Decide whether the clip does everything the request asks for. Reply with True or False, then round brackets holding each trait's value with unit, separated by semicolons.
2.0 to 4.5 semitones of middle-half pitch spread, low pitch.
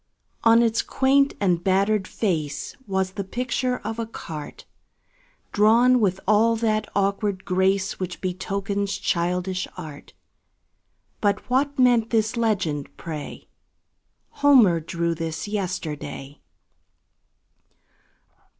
False (4.0 semitones; 200 Hz)